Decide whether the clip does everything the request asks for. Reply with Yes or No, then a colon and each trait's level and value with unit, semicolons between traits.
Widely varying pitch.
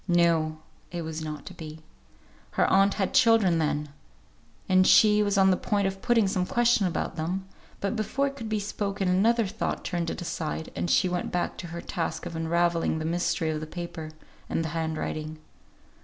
No: average, 3.6 semitones